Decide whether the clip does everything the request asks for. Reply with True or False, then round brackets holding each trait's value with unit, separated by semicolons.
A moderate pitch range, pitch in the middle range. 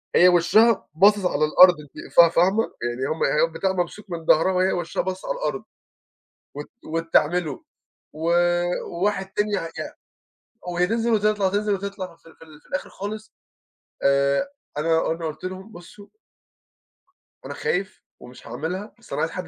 True (3.7 semitones; 180 Hz)